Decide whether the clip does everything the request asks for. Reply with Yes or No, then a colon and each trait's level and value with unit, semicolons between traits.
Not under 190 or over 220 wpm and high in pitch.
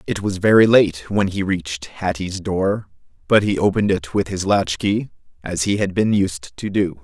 No: fast, 205 wpm; very low, 95 Hz